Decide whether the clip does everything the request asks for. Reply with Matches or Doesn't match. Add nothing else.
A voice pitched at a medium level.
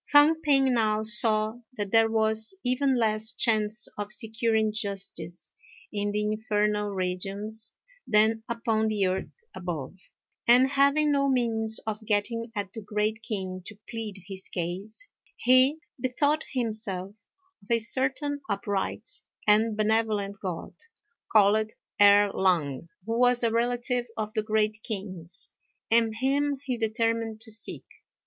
Doesn't match